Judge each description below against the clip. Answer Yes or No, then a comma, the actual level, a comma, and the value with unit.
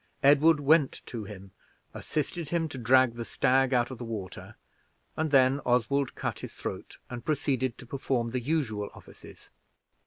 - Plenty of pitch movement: No, average, 3.4 semitones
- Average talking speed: Yes, average, 160 wpm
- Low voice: Yes, low, 130 Hz